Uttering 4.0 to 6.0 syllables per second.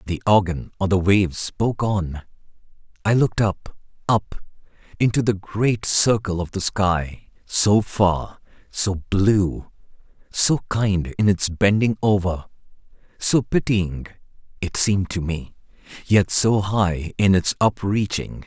No: 3.8 syllables/s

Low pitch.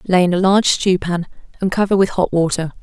No: medium, 185 Hz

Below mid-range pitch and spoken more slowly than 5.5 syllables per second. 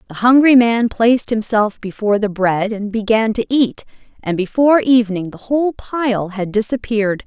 No: high, 225 Hz; 5.1 syllables/s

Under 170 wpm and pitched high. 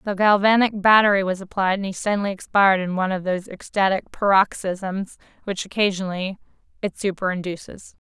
Yes: average, 140 wpm; high, 195 Hz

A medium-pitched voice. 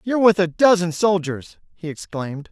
Yes: medium, 180 Hz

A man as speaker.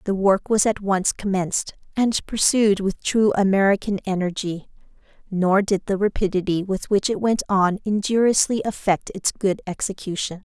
No: female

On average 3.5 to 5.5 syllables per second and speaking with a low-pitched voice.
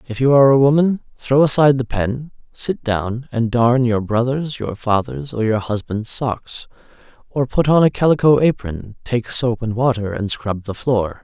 Yes: 4.6 syllables/s; low, 120 Hz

